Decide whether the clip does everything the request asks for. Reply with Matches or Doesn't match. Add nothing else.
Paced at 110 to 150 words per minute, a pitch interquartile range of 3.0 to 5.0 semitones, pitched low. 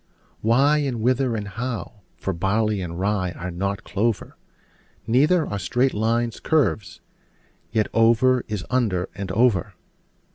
Matches